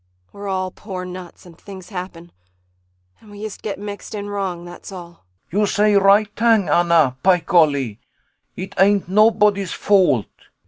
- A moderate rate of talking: Yes, average, 165 wpm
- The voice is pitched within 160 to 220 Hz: Yes, high, 190 Hz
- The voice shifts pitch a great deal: No, average, 2.7 semitones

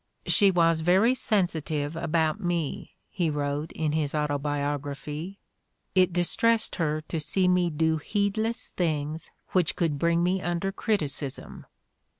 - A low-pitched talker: No, medium, 165 Hz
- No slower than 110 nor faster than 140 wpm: Yes, slow, 135 wpm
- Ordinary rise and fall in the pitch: Yes, average, 3.5 semitones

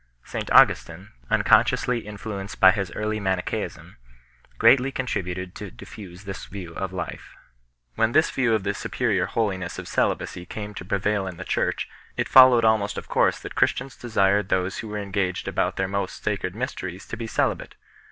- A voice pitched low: Yes, low, 100 Hz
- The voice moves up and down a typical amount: Yes, average, 3.0 semitones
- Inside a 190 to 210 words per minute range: No, average, 175 wpm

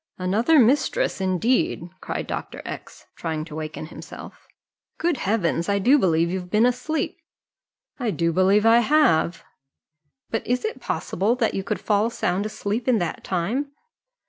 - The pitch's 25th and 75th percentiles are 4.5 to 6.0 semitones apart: Yes, wide, 5.6 semitones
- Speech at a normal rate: Yes, average, 150 wpm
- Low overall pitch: No, high, 210 Hz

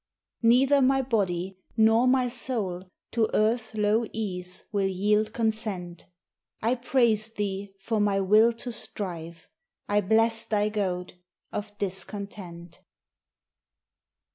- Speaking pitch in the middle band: No, high, 210 Hz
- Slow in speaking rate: Yes, slow, 115 wpm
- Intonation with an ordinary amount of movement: Yes, average, 3.0 semitones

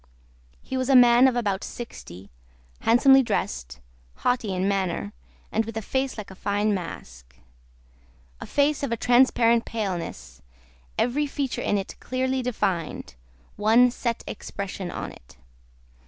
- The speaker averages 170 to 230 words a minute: No, average, 140 wpm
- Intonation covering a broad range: No, average, 4.7 semitones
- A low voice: No, high, 225 Hz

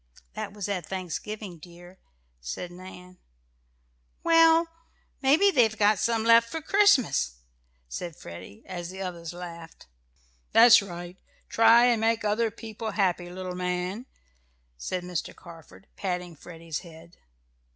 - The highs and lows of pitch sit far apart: No, average, 4.4 semitones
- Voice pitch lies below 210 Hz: Yes, medium, 185 Hz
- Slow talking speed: Yes, slow, 125 wpm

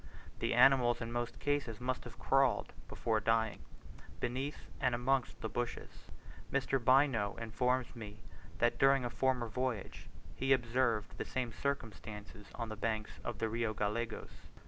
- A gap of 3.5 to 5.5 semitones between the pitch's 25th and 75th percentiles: No, narrow, 2.6 semitones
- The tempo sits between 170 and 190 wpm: No, average, 145 wpm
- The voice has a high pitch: No, low, 120 Hz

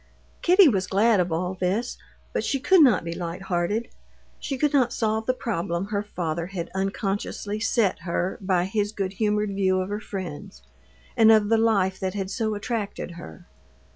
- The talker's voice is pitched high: Yes, high, 200 Hz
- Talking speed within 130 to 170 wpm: No, average, 180 wpm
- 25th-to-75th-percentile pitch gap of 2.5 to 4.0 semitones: Yes, average, 3.2 semitones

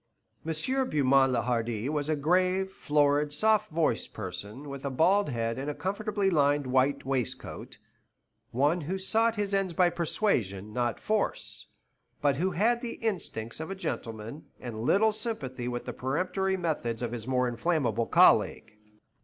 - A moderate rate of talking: Yes, average, 155 wpm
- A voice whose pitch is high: No, medium, 145 Hz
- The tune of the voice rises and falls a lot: Yes, wide, 7.4 semitones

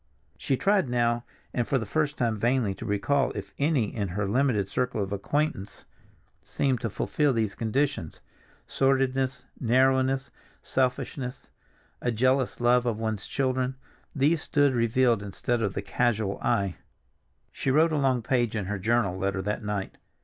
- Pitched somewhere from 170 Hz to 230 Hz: No, low, 120 Hz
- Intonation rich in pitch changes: No, average, 4.3 semitones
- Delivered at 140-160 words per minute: Yes, average, 155 wpm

